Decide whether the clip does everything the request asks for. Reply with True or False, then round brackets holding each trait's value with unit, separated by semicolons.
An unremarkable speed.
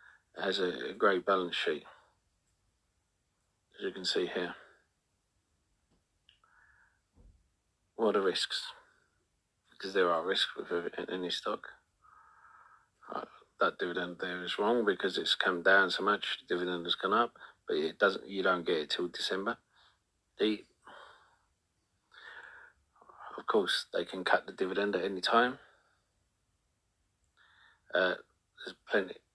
False (120 wpm)